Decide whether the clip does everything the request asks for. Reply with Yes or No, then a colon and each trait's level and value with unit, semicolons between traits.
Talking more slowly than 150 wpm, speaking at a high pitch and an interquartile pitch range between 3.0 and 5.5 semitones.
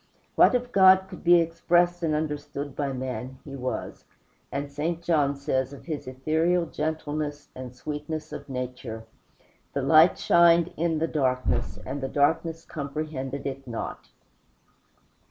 No: average, 140 wpm; medium, 150 Hz; average, 3.7 semitones